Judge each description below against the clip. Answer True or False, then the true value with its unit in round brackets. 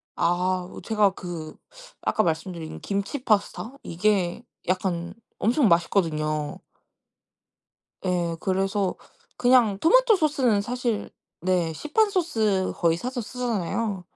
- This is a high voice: True (195 Hz)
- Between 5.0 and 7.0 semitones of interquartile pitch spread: True (5.3 semitones)